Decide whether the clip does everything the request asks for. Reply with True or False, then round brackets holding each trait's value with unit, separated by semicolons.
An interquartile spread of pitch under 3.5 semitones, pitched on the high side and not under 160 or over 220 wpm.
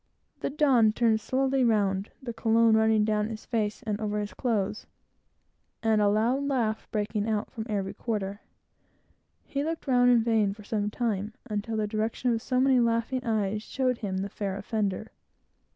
True (2.5 semitones; 220 Hz; 170 wpm)